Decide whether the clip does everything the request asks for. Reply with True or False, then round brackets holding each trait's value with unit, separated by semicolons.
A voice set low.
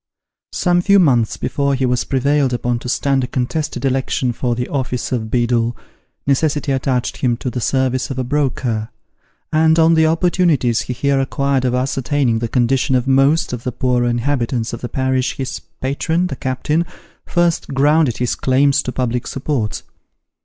True (130 Hz)